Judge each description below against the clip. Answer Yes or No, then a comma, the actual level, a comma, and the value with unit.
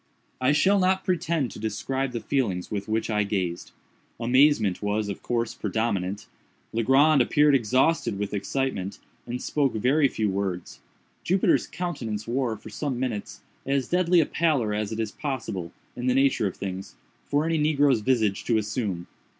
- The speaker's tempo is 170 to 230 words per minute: No, average, 160 wpm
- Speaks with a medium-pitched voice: No, low, 120 Hz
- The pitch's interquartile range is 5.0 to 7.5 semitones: Yes, average, 5.3 semitones